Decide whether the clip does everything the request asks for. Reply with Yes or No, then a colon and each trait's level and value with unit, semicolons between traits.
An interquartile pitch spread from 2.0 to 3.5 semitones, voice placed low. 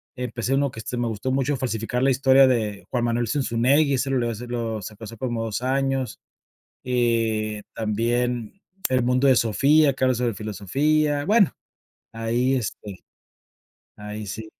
Yes: average, 2.9 semitones; low, 120 Hz